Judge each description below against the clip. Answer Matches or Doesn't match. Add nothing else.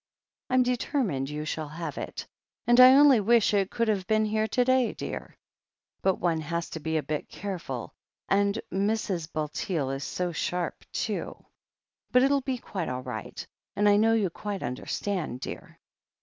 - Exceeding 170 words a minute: Matches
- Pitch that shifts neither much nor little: Doesn't match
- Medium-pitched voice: Doesn't match